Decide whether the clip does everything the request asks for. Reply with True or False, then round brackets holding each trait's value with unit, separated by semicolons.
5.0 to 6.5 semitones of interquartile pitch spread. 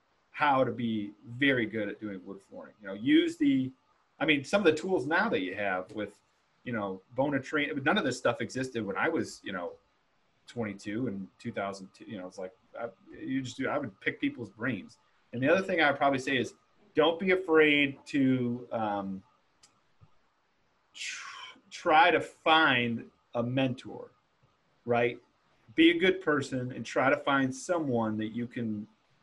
True (5.3 semitones)